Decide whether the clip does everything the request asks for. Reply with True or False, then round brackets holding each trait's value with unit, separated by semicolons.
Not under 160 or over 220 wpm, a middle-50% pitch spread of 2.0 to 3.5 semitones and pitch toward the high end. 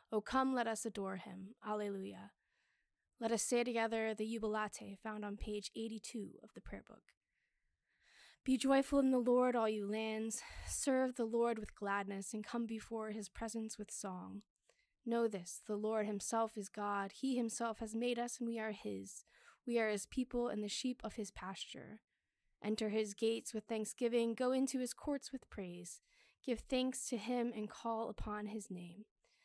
True (175 wpm; 2.5 semitones; 225 Hz)